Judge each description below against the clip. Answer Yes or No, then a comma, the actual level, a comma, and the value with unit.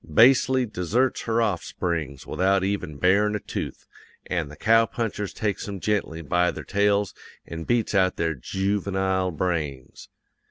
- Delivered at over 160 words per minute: No, average, 145 wpm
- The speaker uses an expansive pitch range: No, average, 3.7 semitones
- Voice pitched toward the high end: No, very low, 95 Hz